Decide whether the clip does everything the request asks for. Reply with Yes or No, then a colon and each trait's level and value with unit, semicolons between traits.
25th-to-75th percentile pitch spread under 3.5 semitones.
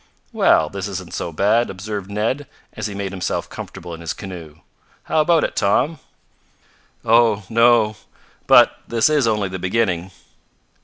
No: average, 3.8 semitones